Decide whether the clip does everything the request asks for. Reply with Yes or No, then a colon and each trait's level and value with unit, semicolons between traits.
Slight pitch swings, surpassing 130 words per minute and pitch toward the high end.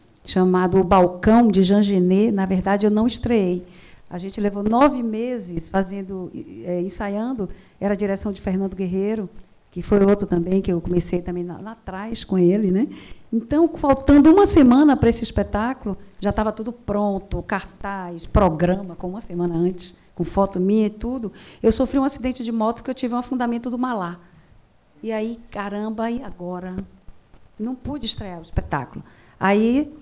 No: average, 3.9 semitones; average, 170 wpm; high, 200 Hz